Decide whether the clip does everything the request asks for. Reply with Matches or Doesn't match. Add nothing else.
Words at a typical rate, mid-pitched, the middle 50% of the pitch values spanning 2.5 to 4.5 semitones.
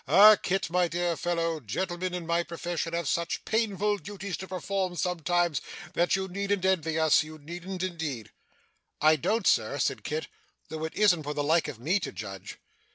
Matches